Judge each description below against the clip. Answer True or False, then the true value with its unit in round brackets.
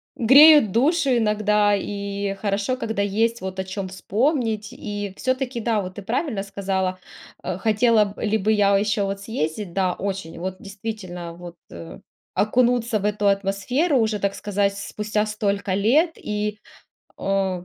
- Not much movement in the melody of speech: True (2.3 semitones)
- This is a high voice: True (205 Hz)